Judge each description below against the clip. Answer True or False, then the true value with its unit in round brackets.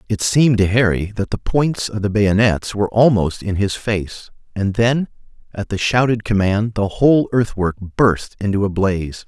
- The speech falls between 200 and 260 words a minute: False (180 wpm)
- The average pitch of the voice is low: True (105 Hz)